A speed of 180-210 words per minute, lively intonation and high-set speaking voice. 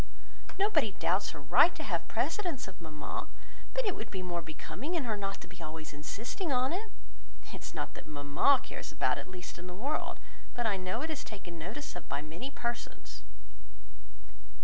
Yes: average, 195 wpm; wide, 8.8 semitones; high, 195 Hz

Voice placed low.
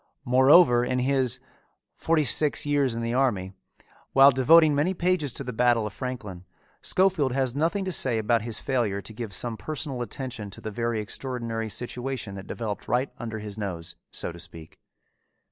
Yes: low, 125 Hz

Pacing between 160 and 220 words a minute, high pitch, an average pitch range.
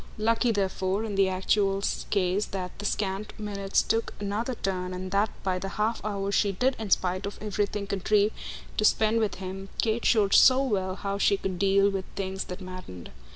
No: average, 190 wpm; high, 200 Hz; narrow, 1.9 semitones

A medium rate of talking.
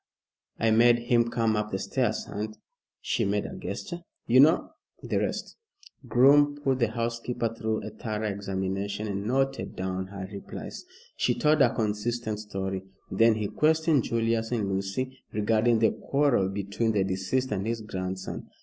Yes: average, 160 wpm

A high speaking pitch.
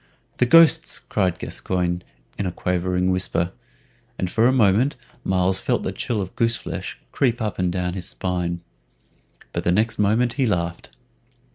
No: very low, 95 Hz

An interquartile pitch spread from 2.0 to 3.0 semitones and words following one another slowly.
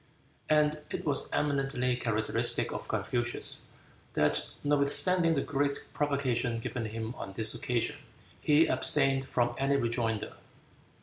No: average, 3.7 semitones; slow, 120 wpm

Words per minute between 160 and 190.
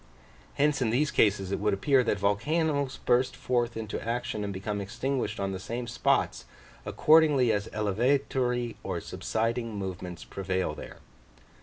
No: average, 145 wpm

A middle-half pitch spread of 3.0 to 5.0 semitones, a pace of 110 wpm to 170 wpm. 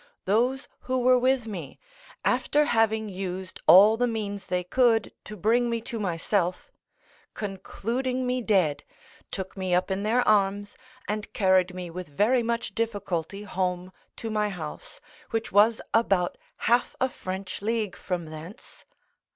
Yes: average, 3.8 semitones; average, 145 wpm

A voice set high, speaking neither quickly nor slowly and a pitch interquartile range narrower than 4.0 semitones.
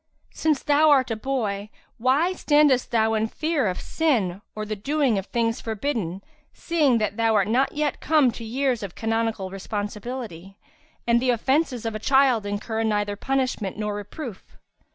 No: high, 230 Hz; average, 165 wpm; average, 4.6 semitones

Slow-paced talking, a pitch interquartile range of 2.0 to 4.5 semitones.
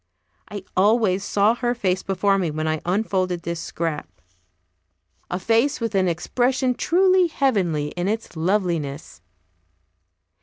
No: slow, 125 wpm; average, 5.0 semitones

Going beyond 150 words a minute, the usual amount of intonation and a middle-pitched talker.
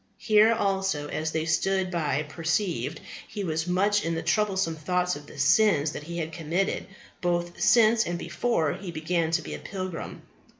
Yes: average, 180 wpm; average, 3.3 semitones; medium, 175 Hz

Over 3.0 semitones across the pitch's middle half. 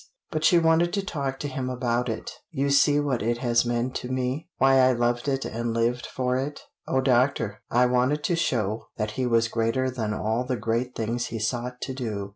No: narrow, 2.4 semitones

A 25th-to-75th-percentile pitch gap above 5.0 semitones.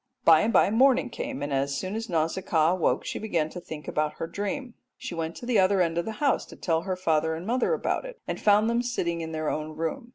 Yes: wide, 5.6 semitones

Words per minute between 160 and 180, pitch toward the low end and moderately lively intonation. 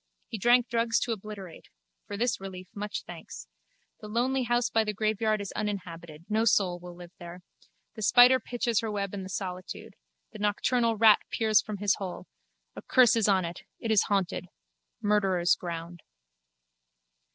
No: average, 165 wpm; high, 205 Hz; average, 3.6 semitones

